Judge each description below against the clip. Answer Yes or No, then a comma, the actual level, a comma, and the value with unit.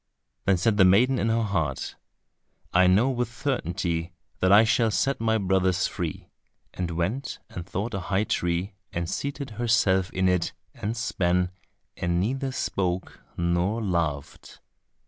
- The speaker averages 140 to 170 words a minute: Yes, average, 145 wpm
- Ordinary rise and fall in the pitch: Yes, average, 4.5 semitones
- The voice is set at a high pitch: No, very low, 95 Hz